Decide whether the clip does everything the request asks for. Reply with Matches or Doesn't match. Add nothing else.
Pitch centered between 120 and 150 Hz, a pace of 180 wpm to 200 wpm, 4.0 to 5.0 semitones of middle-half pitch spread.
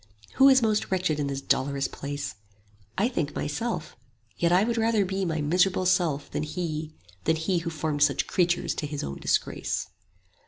Doesn't match